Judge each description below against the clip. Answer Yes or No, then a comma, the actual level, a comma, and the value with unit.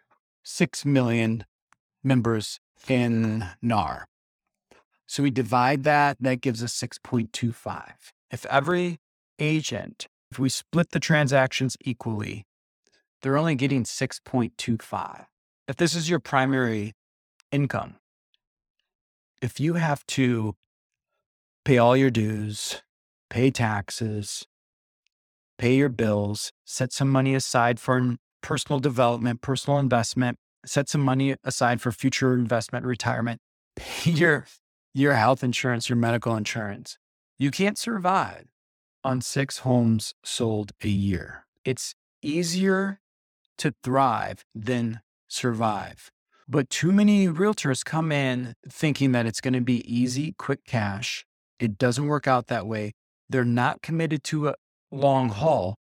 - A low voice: Yes, low, 125 Hz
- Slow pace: Yes, slow, 120 wpm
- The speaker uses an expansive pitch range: No, average, 3.5 semitones